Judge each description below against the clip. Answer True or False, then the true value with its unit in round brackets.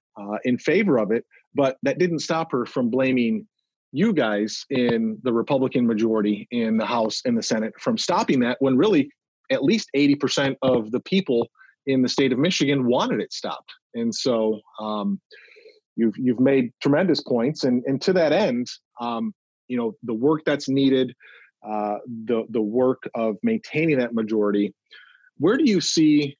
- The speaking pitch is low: True (130 Hz)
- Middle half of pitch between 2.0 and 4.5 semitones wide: False (5.1 semitones)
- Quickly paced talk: False (175 wpm)